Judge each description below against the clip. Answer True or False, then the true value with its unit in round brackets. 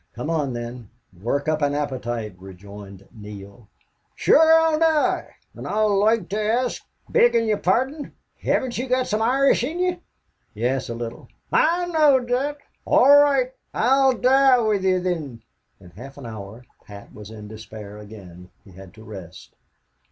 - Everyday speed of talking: True (160 wpm)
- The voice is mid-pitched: True (155 Hz)